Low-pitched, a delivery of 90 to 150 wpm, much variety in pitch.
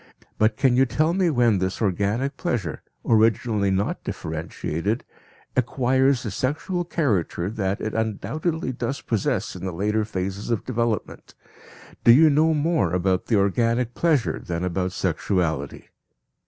Yes: low, 110 Hz; average, 140 wpm; wide, 5.7 semitones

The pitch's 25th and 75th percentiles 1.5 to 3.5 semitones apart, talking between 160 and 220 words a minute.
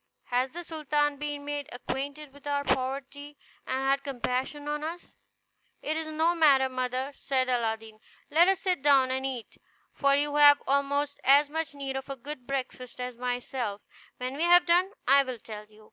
Yes: narrow, 2.4 semitones; average, 180 wpm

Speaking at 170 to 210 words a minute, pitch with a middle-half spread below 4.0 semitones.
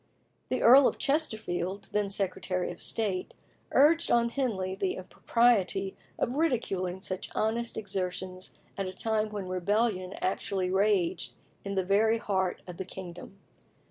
No: average, 140 wpm; average, 3.4 semitones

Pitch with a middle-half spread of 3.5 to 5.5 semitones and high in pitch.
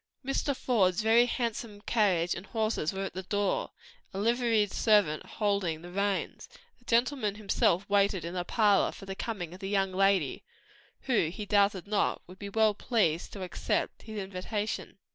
No: average, 2.8 semitones; high, 200 Hz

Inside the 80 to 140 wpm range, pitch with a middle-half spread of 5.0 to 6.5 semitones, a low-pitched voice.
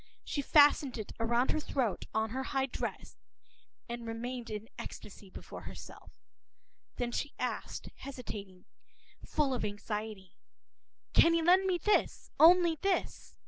No: slow, 135 wpm; wide, 5.5 semitones; very high, 250 Hz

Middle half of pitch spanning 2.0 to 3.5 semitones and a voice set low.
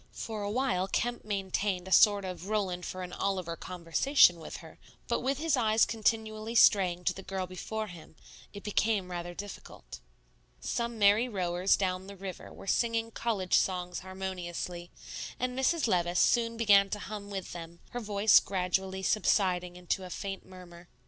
No: average, 3.2 semitones; high, 195 Hz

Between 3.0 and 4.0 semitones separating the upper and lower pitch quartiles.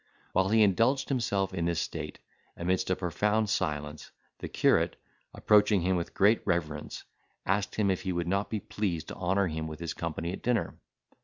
Yes: average, 3.4 semitones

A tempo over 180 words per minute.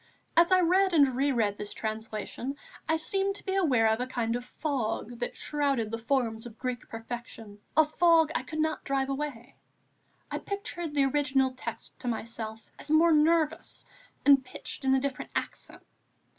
No: average, 175 wpm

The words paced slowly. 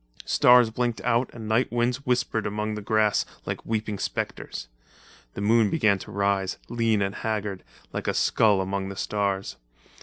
No: average, 160 wpm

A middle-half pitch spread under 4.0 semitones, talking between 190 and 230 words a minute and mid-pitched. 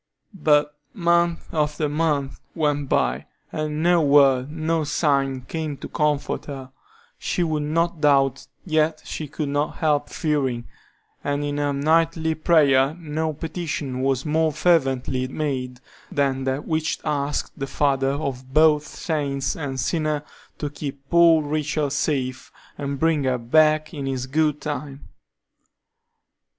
No: narrow, 2.4 semitones; slow, 135 wpm; medium, 150 Hz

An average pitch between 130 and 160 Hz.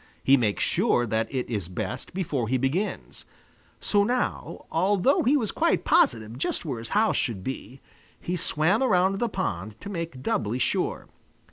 Yes: medium, 140 Hz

